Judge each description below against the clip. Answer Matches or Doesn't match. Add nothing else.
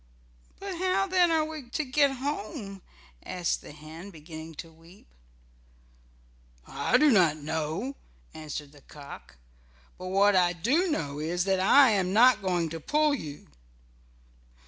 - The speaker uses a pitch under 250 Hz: Matches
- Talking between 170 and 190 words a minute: Doesn't match